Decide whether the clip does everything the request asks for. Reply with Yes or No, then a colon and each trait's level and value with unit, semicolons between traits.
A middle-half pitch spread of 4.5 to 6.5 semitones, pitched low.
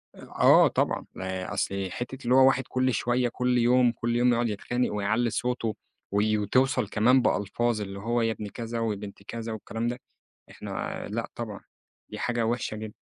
No: average, 2.7 semitones; low, 115 Hz